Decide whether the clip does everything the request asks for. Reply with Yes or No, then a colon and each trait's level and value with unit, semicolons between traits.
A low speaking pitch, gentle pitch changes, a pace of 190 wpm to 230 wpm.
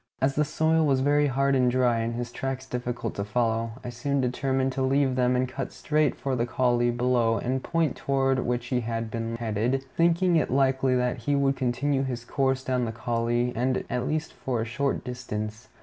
Yes: low, 125 Hz; narrow, 2.2 semitones; average, 200 wpm